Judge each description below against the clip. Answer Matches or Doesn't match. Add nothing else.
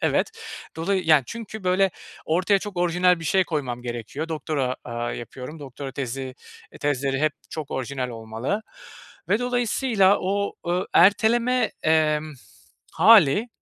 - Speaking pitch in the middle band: Matches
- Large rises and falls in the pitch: Matches